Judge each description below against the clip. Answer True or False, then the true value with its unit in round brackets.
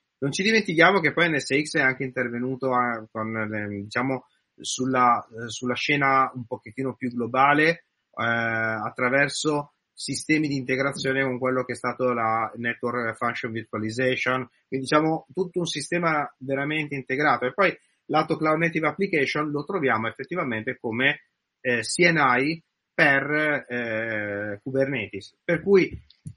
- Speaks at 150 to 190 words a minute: False (125 wpm)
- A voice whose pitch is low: True (130 Hz)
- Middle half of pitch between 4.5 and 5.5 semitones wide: False (4.0 semitones)